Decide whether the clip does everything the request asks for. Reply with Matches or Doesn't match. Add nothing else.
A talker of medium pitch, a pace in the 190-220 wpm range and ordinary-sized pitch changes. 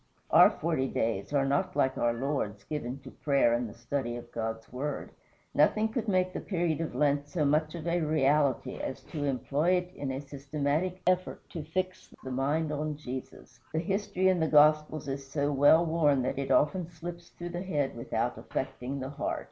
Matches